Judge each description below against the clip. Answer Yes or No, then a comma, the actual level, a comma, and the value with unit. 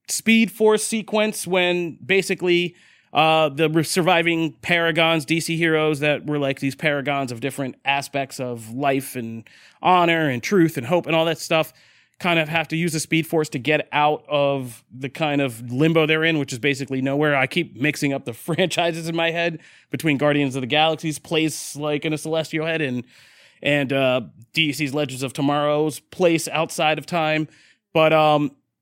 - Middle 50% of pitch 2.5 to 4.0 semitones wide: Yes, average, 2.9 semitones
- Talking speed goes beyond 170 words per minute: Yes, average, 180 wpm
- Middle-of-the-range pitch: Yes, medium, 155 Hz